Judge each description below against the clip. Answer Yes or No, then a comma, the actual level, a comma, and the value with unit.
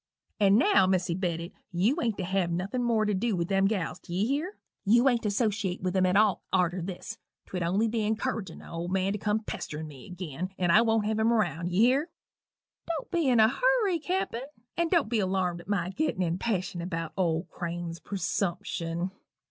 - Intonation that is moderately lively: Yes, average, 4.5 semitones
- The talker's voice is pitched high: Yes, high, 195 Hz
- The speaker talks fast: Yes, fast, 210 wpm